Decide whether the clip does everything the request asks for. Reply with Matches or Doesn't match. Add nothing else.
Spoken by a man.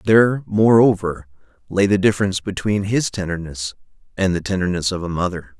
Matches